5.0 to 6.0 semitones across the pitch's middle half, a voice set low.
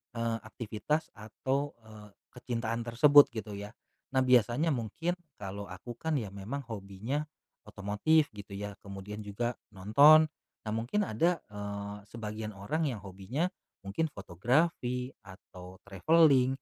Yes: wide, 5.4 semitones; low, 115 Hz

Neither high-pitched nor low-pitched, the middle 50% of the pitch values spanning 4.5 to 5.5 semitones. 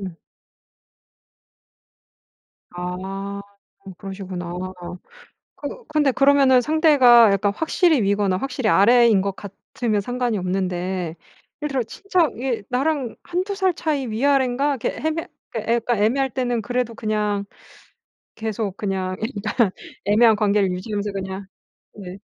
No: high, 220 Hz; average, 5.2 semitones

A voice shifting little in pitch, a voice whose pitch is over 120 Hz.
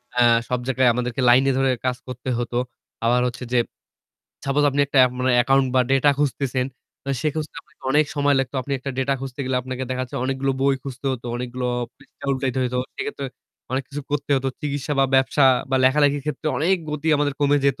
Yes: narrow, 2.0 semitones; low, 135 Hz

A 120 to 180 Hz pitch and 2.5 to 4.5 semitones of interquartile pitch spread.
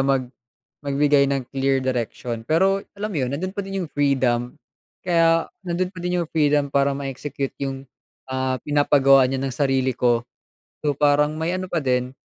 Yes: medium, 140 Hz; average, 3.5 semitones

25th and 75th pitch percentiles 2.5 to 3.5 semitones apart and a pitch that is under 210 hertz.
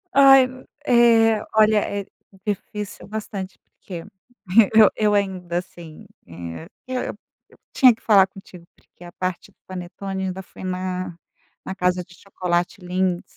Yes: average, 2.8 semitones; high, 190 Hz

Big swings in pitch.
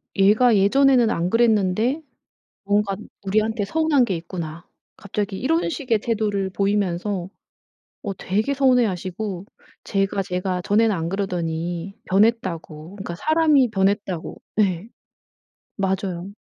No: average, 3.6 semitones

